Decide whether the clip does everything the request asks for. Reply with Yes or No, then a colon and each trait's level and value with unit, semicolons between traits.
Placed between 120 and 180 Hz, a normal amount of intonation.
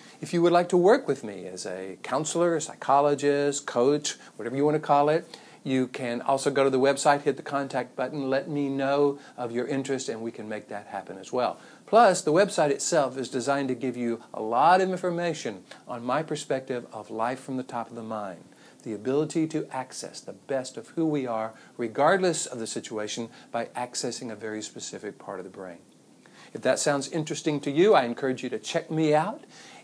Yes: low, 135 Hz; average, 3.9 semitones